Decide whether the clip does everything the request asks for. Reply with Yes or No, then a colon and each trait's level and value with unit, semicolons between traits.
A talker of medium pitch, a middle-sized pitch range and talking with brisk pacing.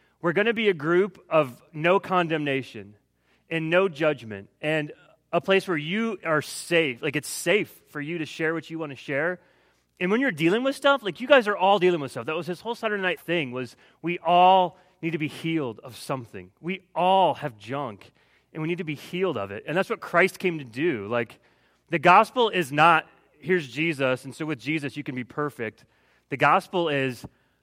Yes: medium, 165 Hz; average, 4.5 semitones; fast, 215 wpm